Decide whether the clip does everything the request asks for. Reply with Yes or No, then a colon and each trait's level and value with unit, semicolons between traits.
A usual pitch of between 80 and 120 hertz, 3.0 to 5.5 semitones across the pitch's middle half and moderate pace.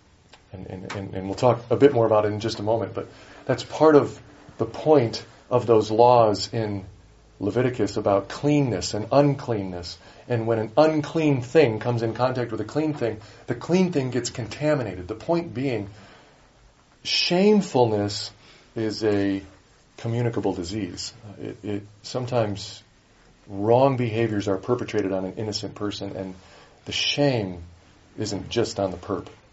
Yes: low, 110 Hz; average, 3.9 semitones; average, 150 wpm